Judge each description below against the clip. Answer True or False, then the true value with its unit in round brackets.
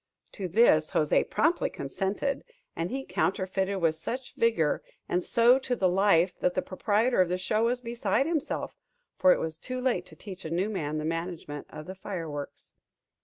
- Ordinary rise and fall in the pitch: False (6.0 semitones)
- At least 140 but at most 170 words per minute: False (180 wpm)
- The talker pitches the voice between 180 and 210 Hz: True (190 Hz)